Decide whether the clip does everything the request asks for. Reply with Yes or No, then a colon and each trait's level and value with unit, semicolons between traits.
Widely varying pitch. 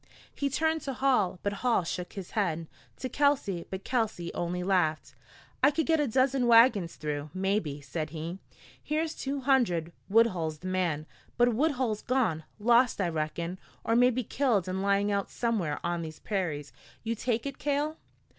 Yes: wide, 6.9 semitones